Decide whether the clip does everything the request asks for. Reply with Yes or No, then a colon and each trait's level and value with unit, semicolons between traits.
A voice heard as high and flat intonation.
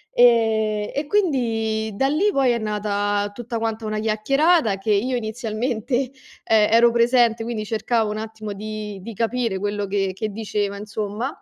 Yes: high, 220 Hz; narrow, 2.3 semitones